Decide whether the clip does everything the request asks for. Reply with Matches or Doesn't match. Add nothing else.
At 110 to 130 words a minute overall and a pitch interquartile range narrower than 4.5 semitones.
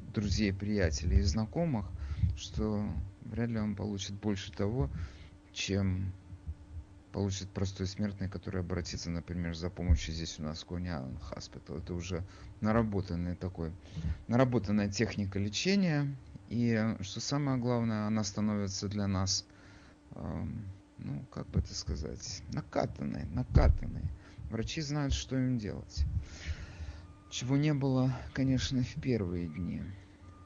Matches